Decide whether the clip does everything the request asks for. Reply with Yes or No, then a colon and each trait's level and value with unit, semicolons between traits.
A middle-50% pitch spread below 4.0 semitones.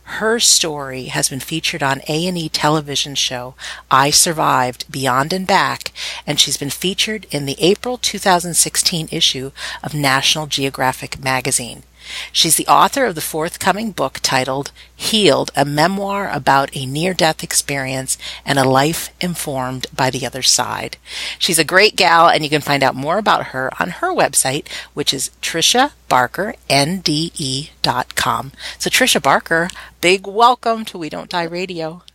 No: average, 4.7 semitones